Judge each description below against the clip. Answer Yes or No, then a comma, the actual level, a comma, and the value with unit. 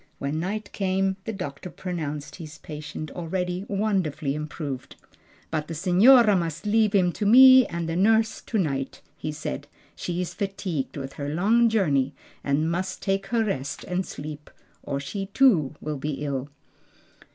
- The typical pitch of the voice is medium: Yes, medium, 175 Hz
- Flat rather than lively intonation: No, average, 4.9 semitones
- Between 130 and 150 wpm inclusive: No, average, 160 wpm